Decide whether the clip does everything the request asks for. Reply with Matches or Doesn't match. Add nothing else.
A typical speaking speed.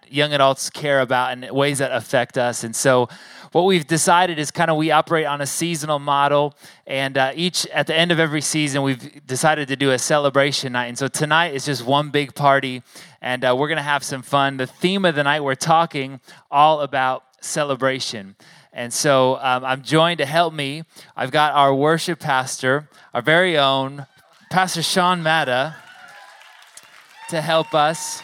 Matches